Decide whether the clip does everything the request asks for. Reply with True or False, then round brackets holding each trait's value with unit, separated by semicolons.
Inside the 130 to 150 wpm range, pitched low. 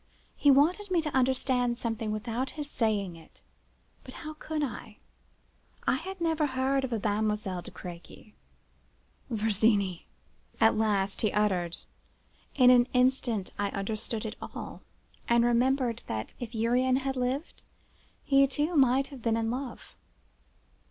False (140 wpm; 240 Hz)